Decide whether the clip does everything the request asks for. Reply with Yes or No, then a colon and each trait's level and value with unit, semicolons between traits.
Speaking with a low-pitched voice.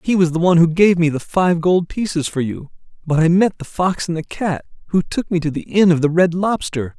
No: medium, 170 Hz